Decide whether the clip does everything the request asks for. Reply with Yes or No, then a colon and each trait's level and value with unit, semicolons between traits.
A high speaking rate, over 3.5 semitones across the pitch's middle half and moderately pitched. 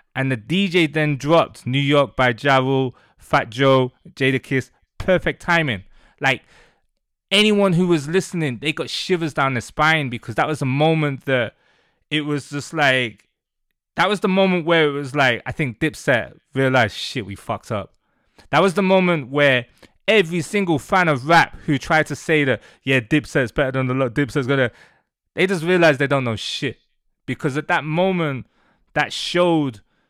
No: average, 175 wpm; average, 4.2 semitones; medium, 145 Hz